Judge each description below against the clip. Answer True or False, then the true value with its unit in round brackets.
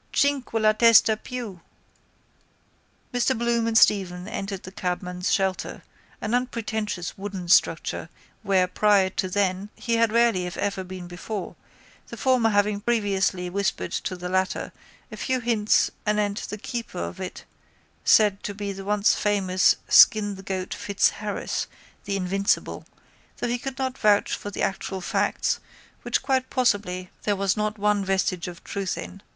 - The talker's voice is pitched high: True (205 Hz)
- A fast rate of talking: False (155 wpm)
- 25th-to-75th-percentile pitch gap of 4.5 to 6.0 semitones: False (2.9 semitones)